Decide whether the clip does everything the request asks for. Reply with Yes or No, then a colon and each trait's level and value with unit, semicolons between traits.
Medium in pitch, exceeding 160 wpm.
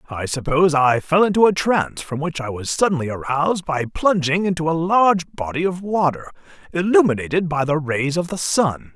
Yes: medium, 160 Hz; average, 190 wpm